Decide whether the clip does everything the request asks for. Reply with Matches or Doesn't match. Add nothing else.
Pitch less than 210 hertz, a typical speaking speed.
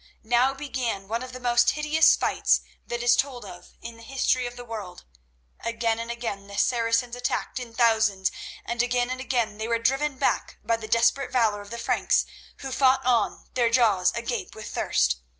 Doesn't match